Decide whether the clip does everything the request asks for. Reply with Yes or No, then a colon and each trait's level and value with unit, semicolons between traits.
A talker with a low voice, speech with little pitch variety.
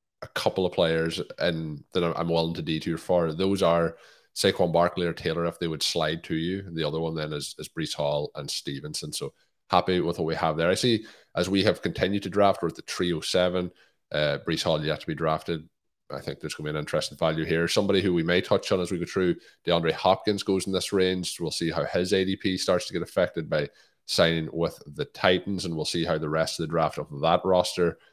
Yes: very low, 85 Hz; narrow, 2.3 semitones